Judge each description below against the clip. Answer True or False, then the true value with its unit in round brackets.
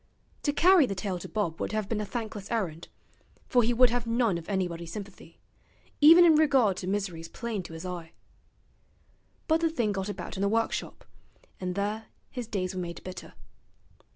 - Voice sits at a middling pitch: False (205 Hz)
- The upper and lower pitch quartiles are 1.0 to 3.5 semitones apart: False (4.5 semitones)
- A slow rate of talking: False (185 wpm)